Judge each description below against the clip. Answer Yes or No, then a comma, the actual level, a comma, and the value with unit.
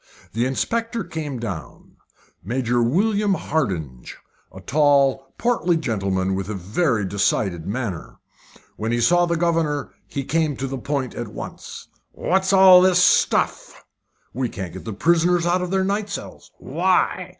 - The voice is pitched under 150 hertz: Yes, medium, 140 Hz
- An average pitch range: No, wide, 8.4 semitones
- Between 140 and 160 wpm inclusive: Yes, average, 150 wpm